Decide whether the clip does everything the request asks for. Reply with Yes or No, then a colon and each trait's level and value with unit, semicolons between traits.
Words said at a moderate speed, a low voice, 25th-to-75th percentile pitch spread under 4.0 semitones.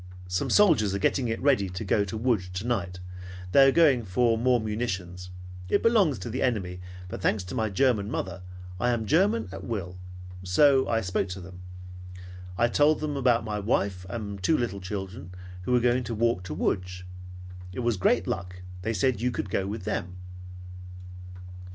No: average, 180 wpm; low, 105 Hz; average, 4.9 semitones